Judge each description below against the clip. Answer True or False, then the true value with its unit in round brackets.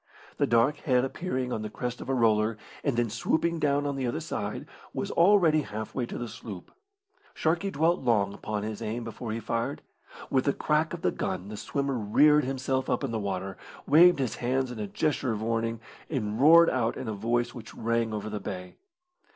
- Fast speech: True (210 wpm)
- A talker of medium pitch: False (120 Hz)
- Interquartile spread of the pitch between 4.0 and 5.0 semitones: True (4.6 semitones)